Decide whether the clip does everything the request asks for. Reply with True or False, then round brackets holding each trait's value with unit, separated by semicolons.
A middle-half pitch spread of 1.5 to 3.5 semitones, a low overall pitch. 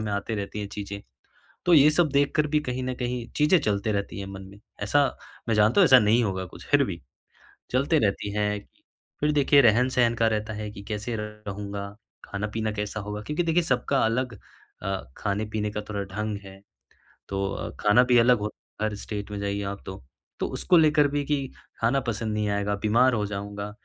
False (3.9 semitones; 105 Hz)